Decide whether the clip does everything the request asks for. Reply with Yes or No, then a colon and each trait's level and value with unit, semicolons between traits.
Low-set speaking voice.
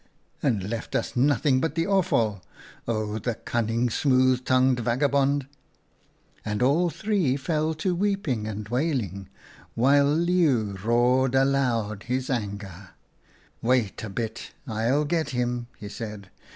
Yes: low, 125 Hz